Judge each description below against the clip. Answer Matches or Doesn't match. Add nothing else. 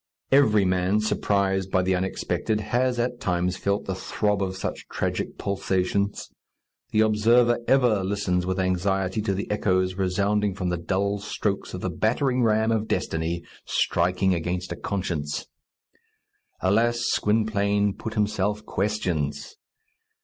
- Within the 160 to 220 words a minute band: Doesn't match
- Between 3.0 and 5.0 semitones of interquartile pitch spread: Doesn't match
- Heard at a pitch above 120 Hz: Doesn't match